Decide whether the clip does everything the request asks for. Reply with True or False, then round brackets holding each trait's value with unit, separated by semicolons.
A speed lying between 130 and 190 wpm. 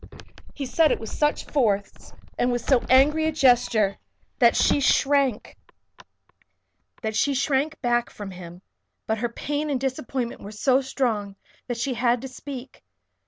True (140 wpm)